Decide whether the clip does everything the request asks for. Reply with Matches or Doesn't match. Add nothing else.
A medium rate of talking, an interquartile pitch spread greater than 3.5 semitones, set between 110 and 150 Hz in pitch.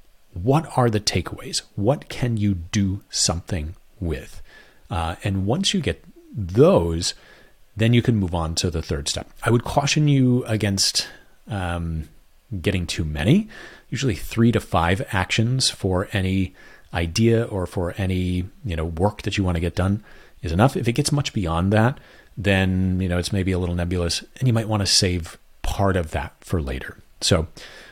Doesn't match